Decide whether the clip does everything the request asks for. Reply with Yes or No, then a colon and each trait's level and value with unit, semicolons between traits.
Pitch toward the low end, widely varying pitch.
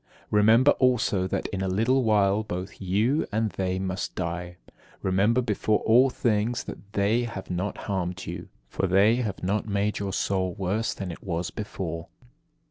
No: low, 100 Hz; average, 3.0 semitones